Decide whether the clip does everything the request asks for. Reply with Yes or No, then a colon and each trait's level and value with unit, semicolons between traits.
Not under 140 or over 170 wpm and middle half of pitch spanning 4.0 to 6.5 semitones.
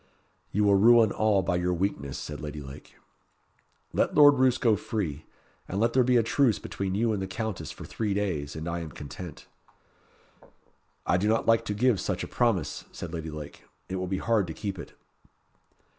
No: average, 195 wpm; average, 5.1 semitones